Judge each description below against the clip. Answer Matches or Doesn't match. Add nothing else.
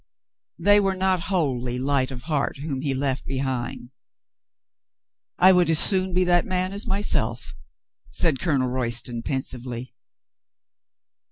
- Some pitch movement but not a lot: Doesn't match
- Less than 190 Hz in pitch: Matches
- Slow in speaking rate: Matches